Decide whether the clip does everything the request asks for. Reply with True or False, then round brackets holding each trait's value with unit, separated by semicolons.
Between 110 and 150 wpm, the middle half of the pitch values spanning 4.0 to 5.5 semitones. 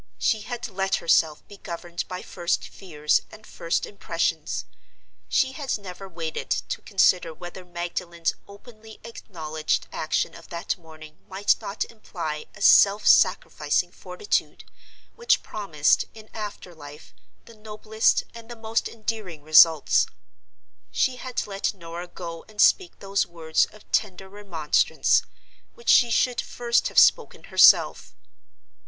True (135 wpm; 4.6 semitones)